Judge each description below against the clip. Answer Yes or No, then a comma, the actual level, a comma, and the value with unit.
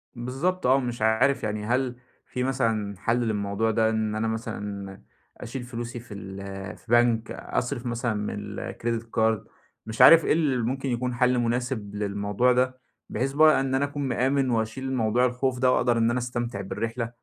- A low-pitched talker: Yes, low, 120 Hz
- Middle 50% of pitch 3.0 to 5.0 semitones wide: No, narrow, 2.5 semitones